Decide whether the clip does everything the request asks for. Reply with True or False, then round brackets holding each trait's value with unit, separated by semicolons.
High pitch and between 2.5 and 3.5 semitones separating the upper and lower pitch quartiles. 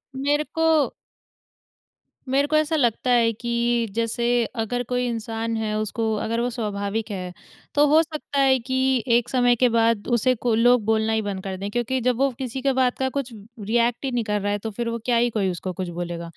True (235 Hz; 2.8 semitones)